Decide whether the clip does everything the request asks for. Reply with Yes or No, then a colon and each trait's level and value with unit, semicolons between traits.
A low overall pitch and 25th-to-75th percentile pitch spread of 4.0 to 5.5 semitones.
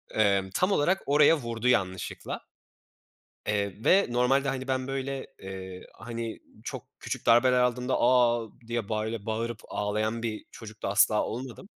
No: low, 115 Hz; average, 3.2 semitones